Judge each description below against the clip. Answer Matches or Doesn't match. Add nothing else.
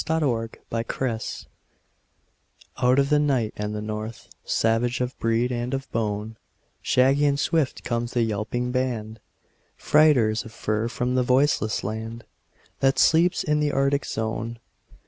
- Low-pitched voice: Matches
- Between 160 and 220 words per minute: Doesn't match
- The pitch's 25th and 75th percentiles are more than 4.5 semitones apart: Doesn't match